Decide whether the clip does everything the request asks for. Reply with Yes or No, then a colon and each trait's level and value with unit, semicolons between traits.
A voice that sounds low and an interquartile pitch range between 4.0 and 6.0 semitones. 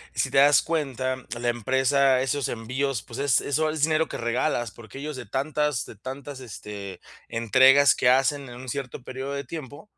No: low, 130 Hz; average, 2.8 semitones